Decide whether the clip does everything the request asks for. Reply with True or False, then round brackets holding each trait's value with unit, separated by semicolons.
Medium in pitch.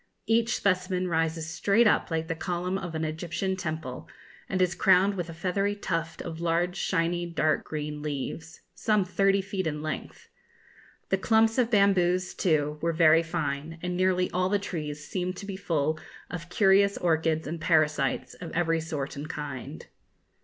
True (170 Hz)